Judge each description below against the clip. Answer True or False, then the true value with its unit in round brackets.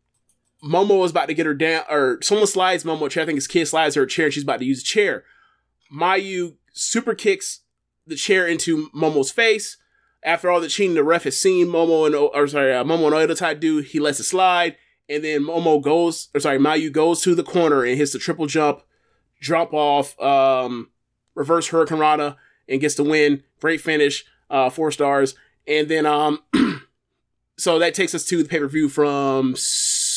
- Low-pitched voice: False (155 Hz)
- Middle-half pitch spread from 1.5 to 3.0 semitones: True (2.7 semitones)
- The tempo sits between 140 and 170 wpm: False (195 wpm)